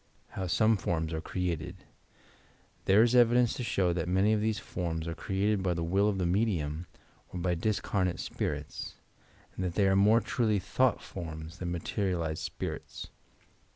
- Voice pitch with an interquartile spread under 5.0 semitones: Yes, average, 3.6 semitones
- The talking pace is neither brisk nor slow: Yes, average, 165 wpm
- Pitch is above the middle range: No, very low, 95 Hz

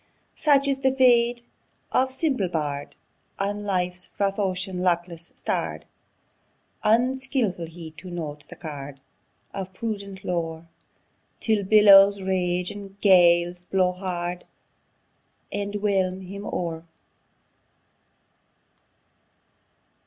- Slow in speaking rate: Yes, slow, 100 wpm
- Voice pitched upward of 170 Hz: Yes, high, 190 Hz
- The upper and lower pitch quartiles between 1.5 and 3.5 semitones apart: Yes, average, 2.9 semitones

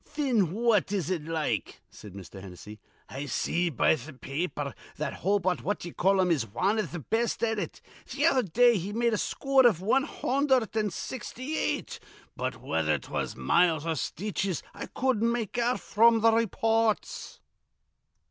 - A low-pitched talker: No, high, 205 Hz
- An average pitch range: No, wide, 6.3 semitones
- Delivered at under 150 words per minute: No, average, 175 wpm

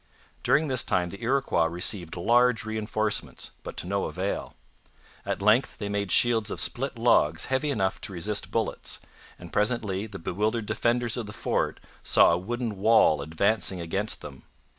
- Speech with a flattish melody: No, average, 4.0 semitones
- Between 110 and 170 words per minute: Yes, average, 160 wpm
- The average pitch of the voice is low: Yes, low, 105 Hz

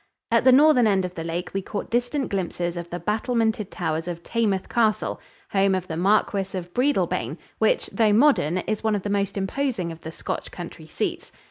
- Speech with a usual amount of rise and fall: Yes, average, 4.4 semitones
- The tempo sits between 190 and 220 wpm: Yes, average, 200 wpm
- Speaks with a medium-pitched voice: No, high, 200 Hz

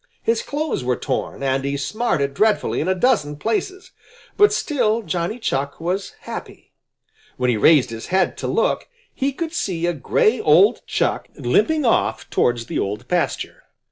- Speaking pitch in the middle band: Yes, medium, 180 Hz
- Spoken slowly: No, average, 165 wpm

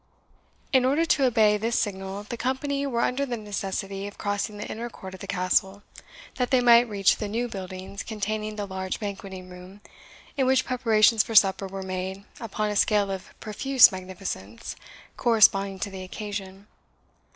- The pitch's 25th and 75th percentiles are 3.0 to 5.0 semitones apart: Yes, average, 3.4 semitones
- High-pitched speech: Yes, high, 205 Hz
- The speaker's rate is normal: Yes, average, 170 wpm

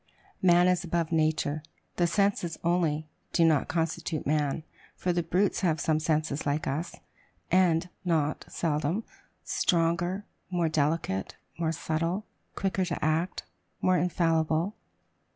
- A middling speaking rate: No, slow, 125 wpm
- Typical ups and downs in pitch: No, narrow, 2.3 semitones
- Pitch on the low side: No, medium, 165 Hz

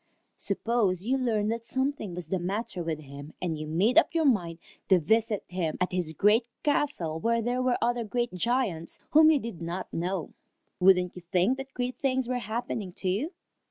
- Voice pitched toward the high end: Yes, high, 210 Hz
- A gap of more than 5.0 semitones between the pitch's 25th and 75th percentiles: Yes, wide, 5.5 semitones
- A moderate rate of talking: Yes, average, 195 wpm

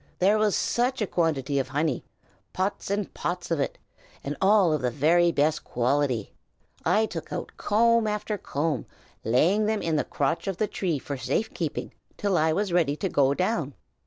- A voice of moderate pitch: Yes, medium, 170 Hz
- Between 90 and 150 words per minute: No, average, 185 wpm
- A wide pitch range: Yes, wide, 6.3 semitones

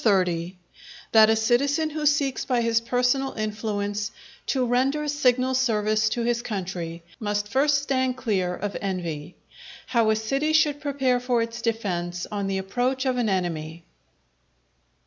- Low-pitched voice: No, high, 230 Hz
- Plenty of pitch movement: No, average, 4.7 semitones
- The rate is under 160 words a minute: Yes, average, 145 wpm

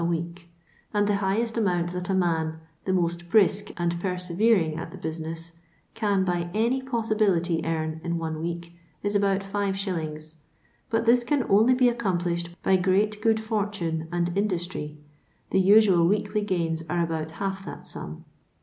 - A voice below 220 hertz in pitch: Yes, medium, 185 Hz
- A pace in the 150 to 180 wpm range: Yes, average, 165 wpm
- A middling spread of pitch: Yes, average, 3.6 semitones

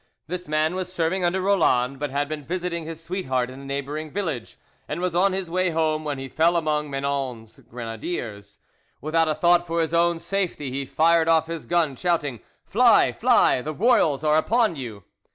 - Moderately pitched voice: Yes, medium, 155 Hz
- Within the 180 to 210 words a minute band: Yes, average, 190 wpm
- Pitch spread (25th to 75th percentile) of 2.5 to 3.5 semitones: No, average, 3.9 semitones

